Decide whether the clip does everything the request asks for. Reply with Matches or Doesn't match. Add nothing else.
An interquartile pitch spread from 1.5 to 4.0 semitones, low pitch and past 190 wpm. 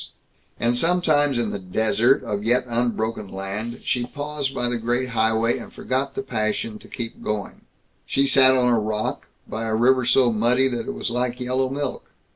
Doesn't match